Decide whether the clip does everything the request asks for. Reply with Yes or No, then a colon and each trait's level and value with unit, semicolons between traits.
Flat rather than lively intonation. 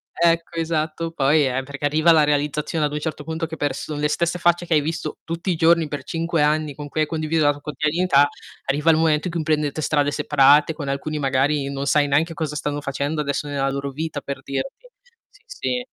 Yes: narrow, 2.1 semitones